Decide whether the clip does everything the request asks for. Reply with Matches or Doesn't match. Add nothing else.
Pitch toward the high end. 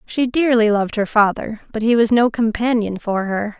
Matches